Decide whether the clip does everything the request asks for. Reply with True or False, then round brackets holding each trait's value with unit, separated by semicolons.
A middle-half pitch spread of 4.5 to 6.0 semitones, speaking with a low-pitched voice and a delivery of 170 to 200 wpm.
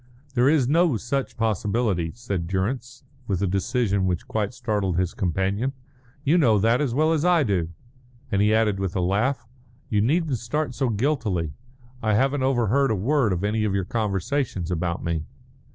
True (5.5 semitones; 110 Hz; 175 wpm)